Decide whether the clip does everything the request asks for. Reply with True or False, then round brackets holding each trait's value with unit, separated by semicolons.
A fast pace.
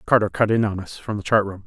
True (325 wpm)